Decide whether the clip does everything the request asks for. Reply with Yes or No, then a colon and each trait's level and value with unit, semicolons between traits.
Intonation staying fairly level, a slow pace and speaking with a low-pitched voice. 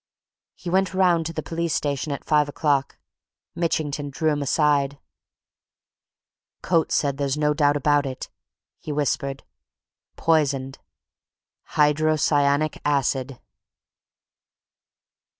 No: narrow, 1.8 semitones; slow, 100 wpm; medium, 145 Hz